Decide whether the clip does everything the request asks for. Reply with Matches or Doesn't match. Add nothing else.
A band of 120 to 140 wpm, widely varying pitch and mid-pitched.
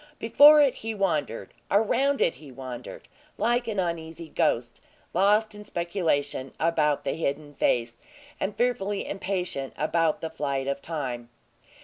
Matches